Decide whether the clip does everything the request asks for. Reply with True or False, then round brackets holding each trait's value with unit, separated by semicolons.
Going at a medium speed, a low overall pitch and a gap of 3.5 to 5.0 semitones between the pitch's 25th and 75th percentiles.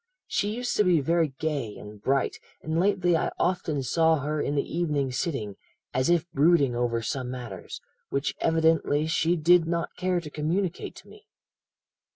False (170 wpm; 160 Hz; 4.2 semitones)